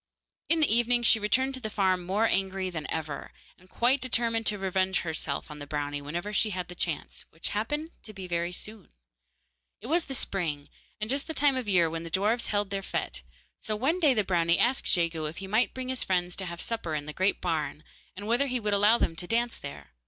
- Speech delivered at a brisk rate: Yes, fast, 230 wpm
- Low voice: No, high, 195 Hz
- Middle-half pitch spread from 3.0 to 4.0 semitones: No, wide, 5.5 semitones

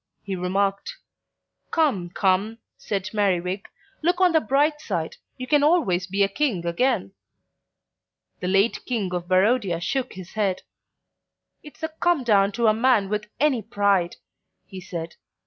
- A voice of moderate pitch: No, high, 205 Hz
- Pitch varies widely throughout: Yes, wide, 5.7 semitones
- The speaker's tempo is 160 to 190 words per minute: No, average, 145 wpm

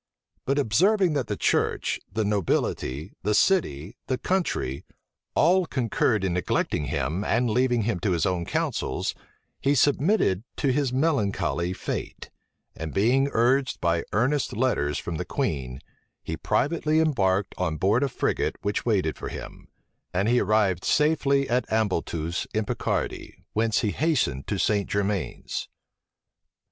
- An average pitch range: No, wide, 7.2 semitones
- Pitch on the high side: No, low, 110 Hz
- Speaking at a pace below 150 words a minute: Yes, average, 140 wpm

